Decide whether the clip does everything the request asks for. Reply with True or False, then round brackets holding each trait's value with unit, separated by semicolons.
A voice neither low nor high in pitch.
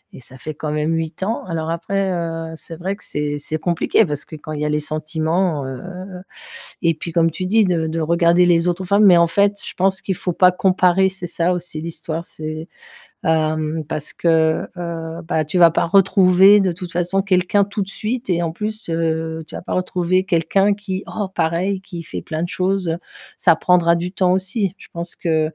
True (170 Hz)